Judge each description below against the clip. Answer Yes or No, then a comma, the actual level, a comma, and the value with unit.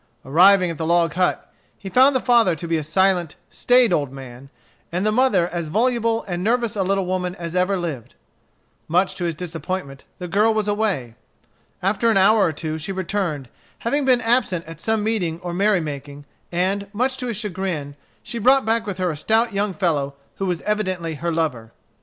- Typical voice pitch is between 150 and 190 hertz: Yes, medium, 185 Hz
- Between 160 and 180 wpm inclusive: No, average, 195 wpm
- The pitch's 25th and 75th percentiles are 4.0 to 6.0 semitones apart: Yes, average, 4.5 semitones